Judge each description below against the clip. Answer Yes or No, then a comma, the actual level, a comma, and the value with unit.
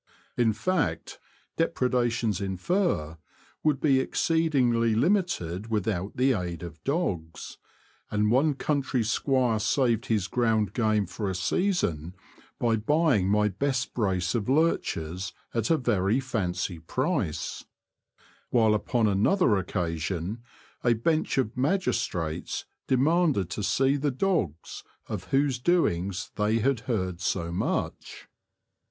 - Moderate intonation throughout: No, wide, 6.4 semitones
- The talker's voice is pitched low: Yes, low, 115 Hz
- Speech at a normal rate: No, slow, 120 wpm